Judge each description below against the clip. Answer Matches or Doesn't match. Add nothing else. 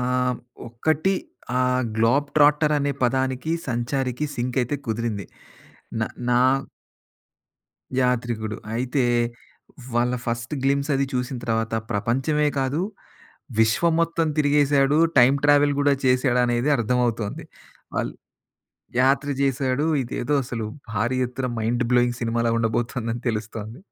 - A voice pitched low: Matches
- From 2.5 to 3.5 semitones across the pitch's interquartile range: Matches